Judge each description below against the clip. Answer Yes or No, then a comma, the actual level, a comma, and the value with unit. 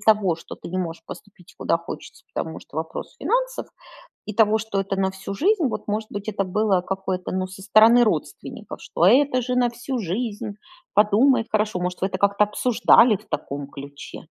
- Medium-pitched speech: No, high, 205 Hz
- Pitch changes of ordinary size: Yes, average, 3.5 semitones